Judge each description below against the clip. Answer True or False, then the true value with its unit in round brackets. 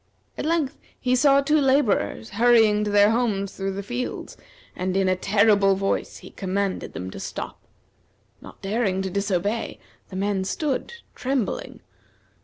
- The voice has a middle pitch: False (205 Hz)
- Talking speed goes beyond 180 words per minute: False (150 wpm)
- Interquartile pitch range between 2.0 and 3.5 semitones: False (4.3 semitones)